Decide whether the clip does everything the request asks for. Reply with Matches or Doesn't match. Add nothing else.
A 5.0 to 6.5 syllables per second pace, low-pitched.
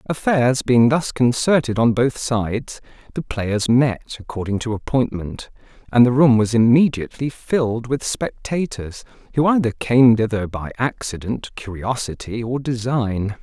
Doesn't match